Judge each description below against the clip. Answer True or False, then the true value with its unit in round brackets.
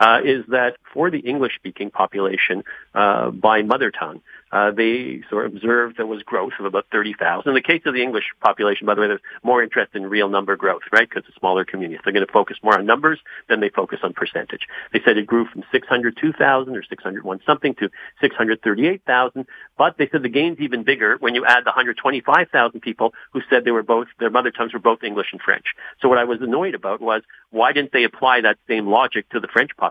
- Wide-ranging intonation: False (4.1 semitones)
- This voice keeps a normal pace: False (230 wpm)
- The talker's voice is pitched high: False (115 Hz)